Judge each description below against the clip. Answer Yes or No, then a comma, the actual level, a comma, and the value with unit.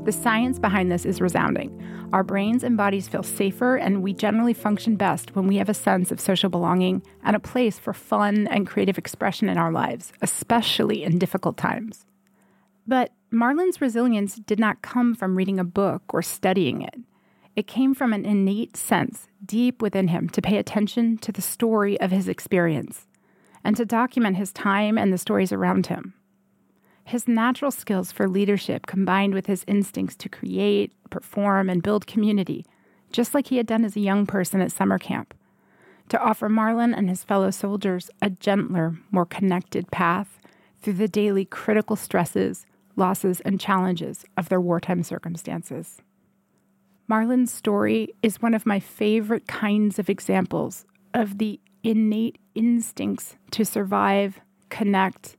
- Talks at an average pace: Yes, average, 160 wpm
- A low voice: No, high, 200 Hz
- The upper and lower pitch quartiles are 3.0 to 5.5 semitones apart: No, narrow, 2.5 semitones